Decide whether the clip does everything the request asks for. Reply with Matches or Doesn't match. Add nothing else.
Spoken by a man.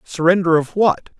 Matches